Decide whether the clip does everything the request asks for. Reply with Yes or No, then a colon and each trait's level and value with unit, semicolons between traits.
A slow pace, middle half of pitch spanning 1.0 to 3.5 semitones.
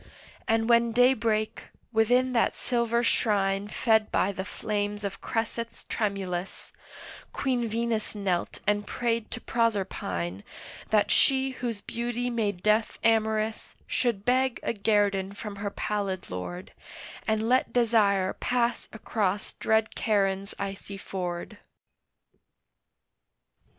Yes: slow, 115 wpm; average, 2.8 semitones